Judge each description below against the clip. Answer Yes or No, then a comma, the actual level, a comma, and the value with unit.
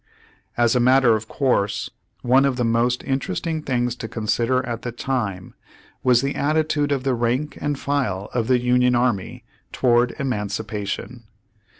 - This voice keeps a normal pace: Yes, average, 160 wpm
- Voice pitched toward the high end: No, low, 125 Hz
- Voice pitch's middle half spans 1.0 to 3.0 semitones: Yes, narrow, 2.6 semitones